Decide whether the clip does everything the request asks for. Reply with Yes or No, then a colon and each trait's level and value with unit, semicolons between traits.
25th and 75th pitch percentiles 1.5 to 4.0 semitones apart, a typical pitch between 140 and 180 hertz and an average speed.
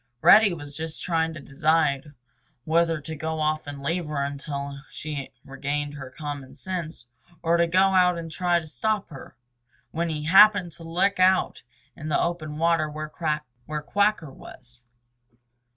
Yes: average, 2.8 semitones; medium, 155 Hz; average, 160 wpm